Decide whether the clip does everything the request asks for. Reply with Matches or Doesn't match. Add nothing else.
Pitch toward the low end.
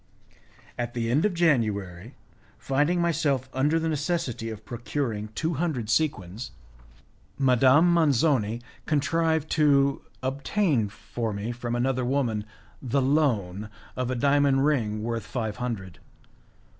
Matches